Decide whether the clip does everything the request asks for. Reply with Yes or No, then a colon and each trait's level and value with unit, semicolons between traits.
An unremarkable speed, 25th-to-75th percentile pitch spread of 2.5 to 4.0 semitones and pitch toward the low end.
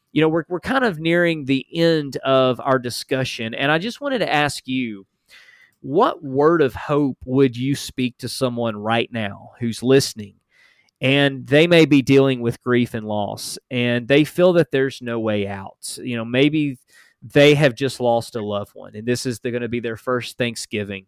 Yes: average, 195 wpm; average, 3.7 semitones; low, 130 Hz